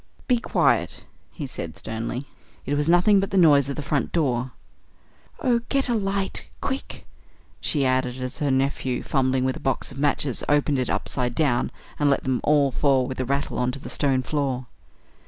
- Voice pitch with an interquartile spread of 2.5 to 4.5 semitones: Yes, average, 2.8 semitones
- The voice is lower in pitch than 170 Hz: Yes, medium, 140 Hz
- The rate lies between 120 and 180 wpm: No, average, 190 wpm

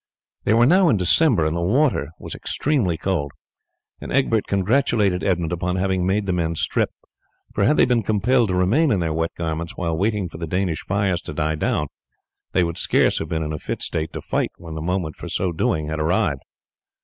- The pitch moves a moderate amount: Yes, average, 4.5 semitones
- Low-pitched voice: Yes, very low, 90 Hz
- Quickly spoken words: Yes, fast, 210 wpm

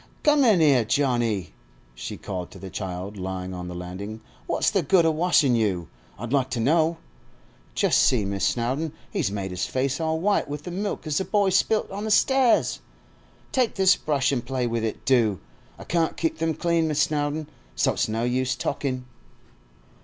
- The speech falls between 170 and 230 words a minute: Yes, average, 190 wpm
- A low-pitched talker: Yes, low, 130 Hz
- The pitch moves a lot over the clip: Yes, wide, 7.4 semitones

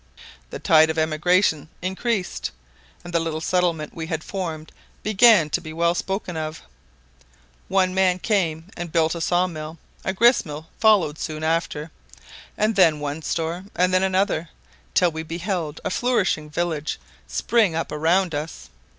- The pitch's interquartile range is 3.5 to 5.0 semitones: No, average, 3.0 semitones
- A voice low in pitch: No, medium, 170 Hz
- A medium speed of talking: Yes, average, 155 wpm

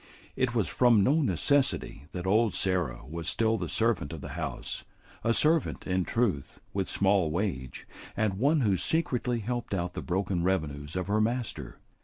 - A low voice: Yes, low, 100 Hz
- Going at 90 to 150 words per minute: No, average, 170 wpm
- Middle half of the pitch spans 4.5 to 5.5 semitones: Yes, average, 5.0 semitones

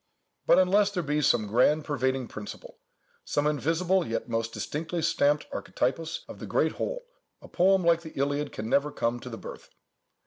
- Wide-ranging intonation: No, average, 4.9 semitones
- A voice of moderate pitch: Yes, medium, 150 Hz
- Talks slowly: No, average, 170 wpm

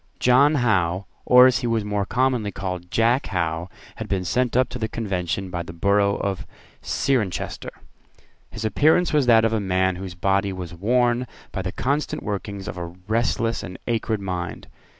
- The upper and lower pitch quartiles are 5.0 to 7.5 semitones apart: No, average, 4.6 semitones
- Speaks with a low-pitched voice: Yes, low, 105 Hz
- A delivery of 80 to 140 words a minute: No, average, 175 wpm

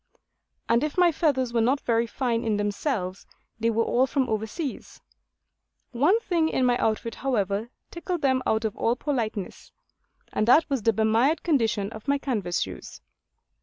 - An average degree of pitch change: Yes, average, 4.2 semitones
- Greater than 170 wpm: No, average, 165 wpm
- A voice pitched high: Yes, high, 235 Hz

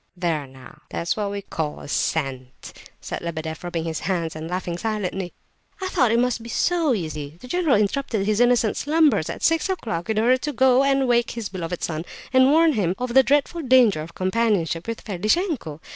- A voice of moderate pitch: No, high, 215 Hz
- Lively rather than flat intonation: Yes, wide, 7.5 semitones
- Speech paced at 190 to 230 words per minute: Yes, average, 200 wpm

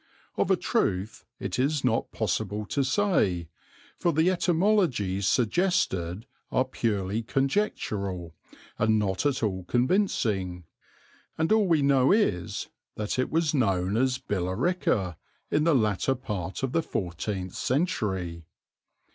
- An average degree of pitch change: No, wide, 7.7 semitones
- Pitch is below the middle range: Yes, low, 110 Hz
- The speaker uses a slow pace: Yes, slow, 125 wpm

